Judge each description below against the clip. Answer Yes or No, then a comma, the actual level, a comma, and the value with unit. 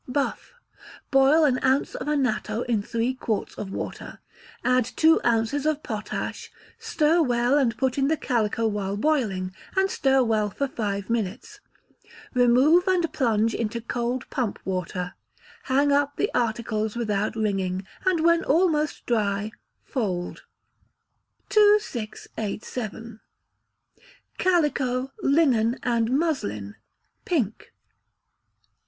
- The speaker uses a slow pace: Yes, slow, 115 wpm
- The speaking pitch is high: Yes, high, 245 Hz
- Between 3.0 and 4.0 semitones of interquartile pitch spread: No, average, 5.1 semitones